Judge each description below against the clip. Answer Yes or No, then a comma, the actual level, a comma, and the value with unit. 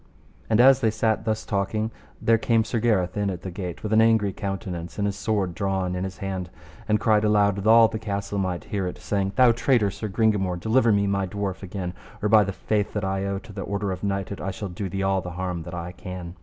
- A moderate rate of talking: No, fast, 245 wpm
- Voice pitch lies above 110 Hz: No, low, 100 Hz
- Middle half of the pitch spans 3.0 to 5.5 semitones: No, narrow, 2.5 semitones